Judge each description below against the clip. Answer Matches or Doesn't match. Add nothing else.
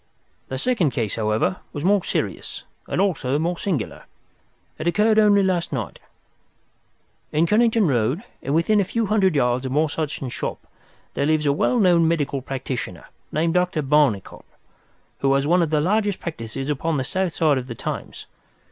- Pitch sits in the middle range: Matches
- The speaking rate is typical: Matches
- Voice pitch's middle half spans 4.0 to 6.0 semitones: Matches